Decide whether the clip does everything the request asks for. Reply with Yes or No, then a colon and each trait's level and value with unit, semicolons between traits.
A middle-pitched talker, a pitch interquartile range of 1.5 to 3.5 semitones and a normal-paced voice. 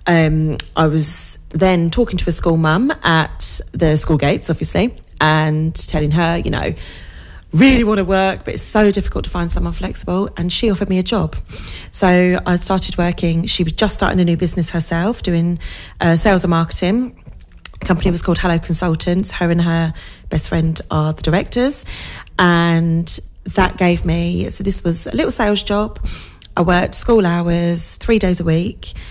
Yes: medium, 175 Hz; average, 2.7 semitones; average, 180 wpm